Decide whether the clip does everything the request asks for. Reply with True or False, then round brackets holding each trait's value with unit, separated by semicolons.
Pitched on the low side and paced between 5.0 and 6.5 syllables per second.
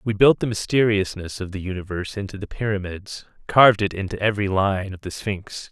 True (100 Hz; 5.8 syllables/s)